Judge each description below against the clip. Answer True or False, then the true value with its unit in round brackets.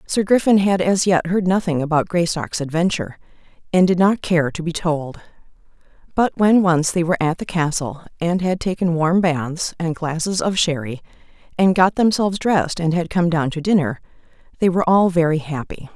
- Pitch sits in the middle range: True (170 Hz)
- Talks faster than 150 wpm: True (185 wpm)